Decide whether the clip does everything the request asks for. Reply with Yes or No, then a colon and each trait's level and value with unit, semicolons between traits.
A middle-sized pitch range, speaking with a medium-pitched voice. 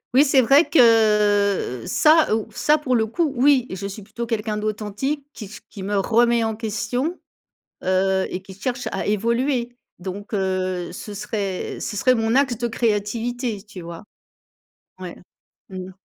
No: average, 3.5 semitones; high, 220 Hz